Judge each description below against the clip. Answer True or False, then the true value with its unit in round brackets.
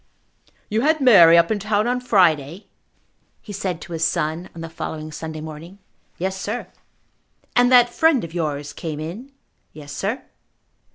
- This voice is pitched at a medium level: True (175 Hz)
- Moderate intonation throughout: False (5.8 semitones)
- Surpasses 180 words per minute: False (160 wpm)